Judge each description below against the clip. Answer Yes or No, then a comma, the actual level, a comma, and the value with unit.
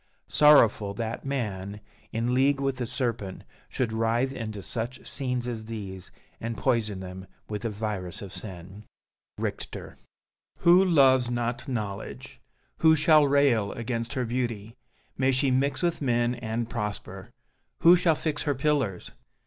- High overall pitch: No, low, 120 Hz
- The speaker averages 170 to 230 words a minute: No, average, 140 wpm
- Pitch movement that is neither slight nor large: Yes, average, 4.1 semitones